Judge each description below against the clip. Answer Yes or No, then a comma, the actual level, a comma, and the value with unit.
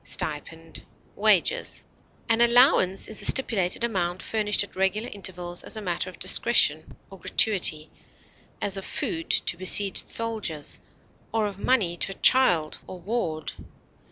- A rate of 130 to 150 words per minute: Yes, slow, 135 wpm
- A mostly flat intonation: No, average, 4.0 semitones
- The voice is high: Yes, high, 195 Hz